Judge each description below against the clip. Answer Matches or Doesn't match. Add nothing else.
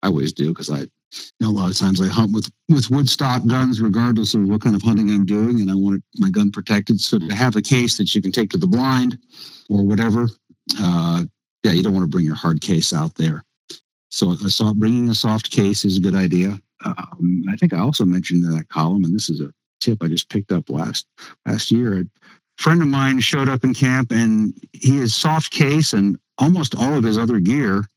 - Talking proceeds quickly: Matches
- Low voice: Matches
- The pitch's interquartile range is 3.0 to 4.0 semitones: Doesn't match